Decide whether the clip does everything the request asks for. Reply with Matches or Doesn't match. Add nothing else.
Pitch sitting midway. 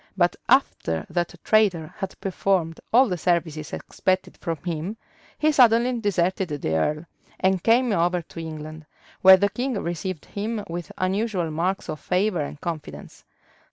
Matches